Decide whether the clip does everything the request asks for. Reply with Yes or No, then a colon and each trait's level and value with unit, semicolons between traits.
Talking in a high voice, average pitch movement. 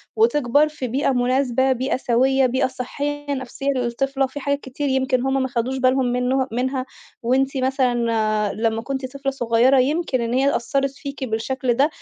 No: very high, 260 Hz; narrow, 1.7 semitones